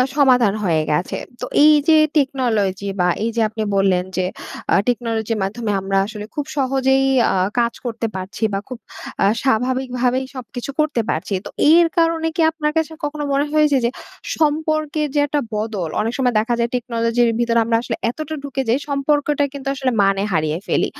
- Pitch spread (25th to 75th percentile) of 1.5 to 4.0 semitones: No, average, 4.7 semitones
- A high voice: Yes, very high, 250 Hz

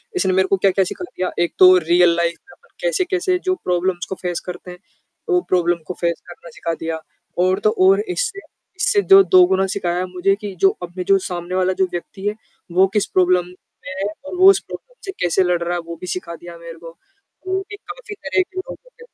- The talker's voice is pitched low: No, medium, 185 Hz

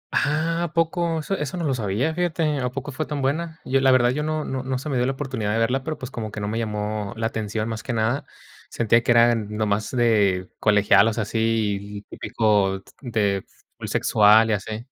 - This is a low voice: Yes, low, 115 Hz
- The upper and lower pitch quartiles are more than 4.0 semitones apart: Yes, average, 4.6 semitones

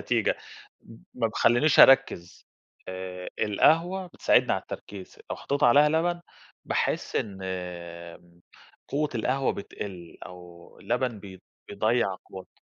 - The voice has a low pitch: Yes, low, 110 Hz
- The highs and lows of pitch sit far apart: Yes, wide, 7.3 semitones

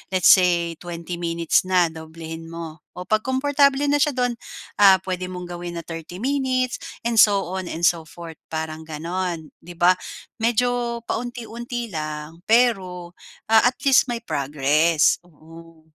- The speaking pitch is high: No, medium, 180 Hz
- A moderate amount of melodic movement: No, wide, 6.1 semitones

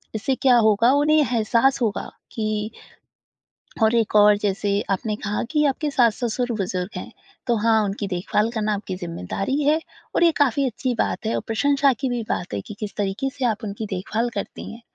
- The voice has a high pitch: Yes, high, 220 Hz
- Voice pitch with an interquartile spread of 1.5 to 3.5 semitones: No, average, 4.0 semitones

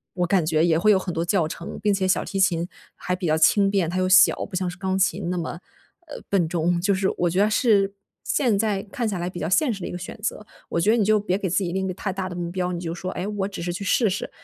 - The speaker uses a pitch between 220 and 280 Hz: No, medium, 185 Hz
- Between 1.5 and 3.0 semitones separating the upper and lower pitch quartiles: Yes, narrow, 2.4 semitones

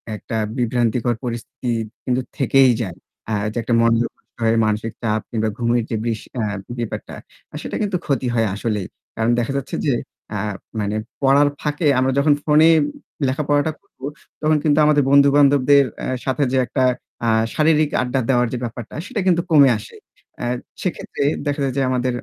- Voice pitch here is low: Yes, low, 130 Hz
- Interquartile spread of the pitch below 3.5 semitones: No, average, 3.8 semitones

